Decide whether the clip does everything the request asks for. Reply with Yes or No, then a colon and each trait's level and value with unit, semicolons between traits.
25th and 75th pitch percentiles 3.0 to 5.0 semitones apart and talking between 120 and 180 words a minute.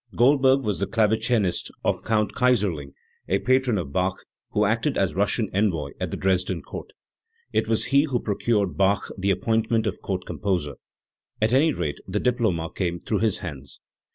Yes: average, 4.1 semitones; average, 175 wpm